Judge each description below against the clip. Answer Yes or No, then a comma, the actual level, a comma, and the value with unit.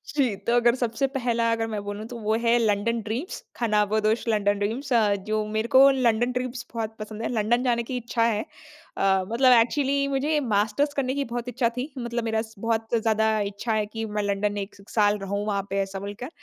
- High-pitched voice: Yes, high, 225 Hz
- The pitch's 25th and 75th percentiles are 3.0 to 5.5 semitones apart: No, narrow, 2.6 semitones